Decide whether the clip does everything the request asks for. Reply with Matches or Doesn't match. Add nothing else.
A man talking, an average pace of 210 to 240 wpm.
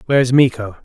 Matches